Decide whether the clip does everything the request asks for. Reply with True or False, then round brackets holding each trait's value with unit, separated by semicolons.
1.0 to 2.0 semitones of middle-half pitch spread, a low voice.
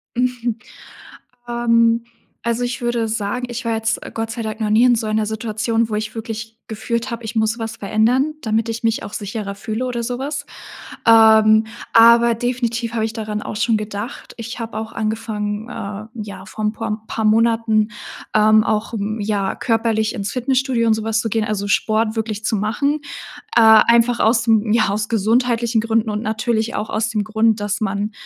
False (1.4 semitones; 225 Hz)